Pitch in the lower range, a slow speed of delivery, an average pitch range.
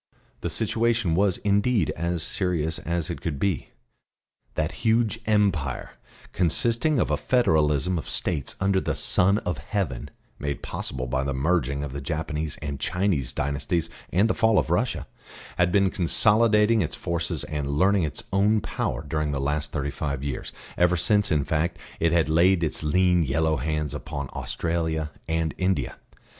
No: very low, 80 Hz; average, 160 wpm; average, 4.7 semitones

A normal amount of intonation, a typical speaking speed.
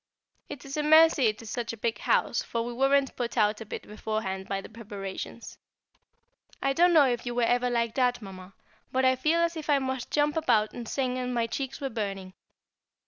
No: average, 3.9 semitones; fast, 215 wpm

